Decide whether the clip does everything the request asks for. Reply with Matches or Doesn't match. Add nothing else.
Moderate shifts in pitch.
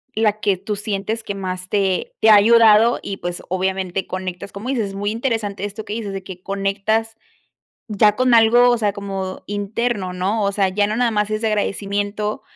Doesn't match